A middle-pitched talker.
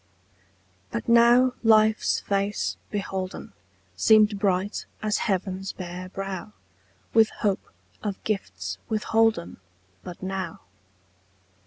No: high, 200 Hz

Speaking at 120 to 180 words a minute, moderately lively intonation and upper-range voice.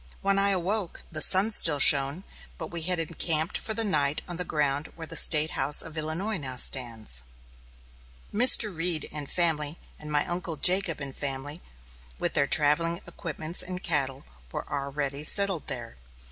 No: average, 165 wpm; average, 3.8 semitones; medium, 155 Hz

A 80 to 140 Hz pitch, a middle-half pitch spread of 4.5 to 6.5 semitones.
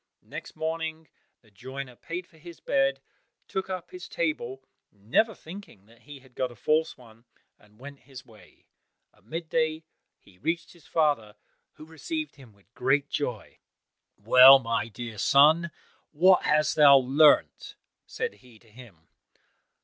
Yes: low, 135 Hz; wide, 5.4 semitones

